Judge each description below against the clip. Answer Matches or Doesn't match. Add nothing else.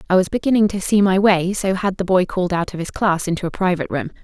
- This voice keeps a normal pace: Doesn't match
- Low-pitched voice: Doesn't match